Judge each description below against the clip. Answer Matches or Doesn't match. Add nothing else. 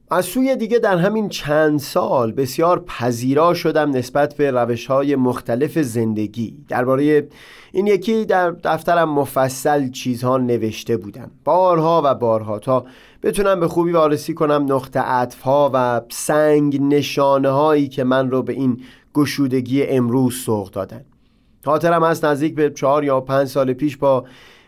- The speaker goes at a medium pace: Matches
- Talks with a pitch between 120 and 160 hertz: Matches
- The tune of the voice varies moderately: Matches